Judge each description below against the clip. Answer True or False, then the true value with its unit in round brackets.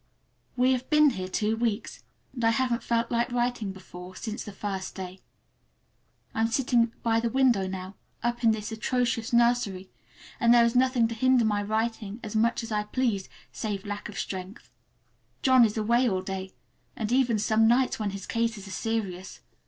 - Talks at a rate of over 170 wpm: True (185 wpm)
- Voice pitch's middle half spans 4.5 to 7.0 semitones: False (2.9 semitones)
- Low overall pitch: False (225 Hz)